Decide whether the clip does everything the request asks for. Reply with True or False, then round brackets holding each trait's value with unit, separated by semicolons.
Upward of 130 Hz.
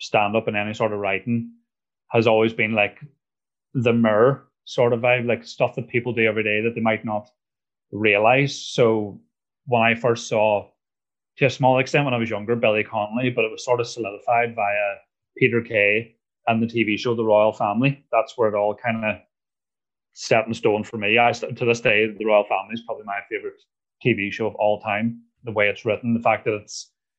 False (115 Hz)